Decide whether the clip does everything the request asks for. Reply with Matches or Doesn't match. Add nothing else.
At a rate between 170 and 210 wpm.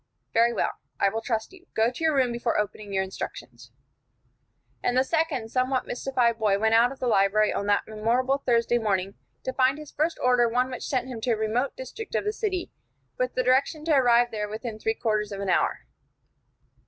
Matches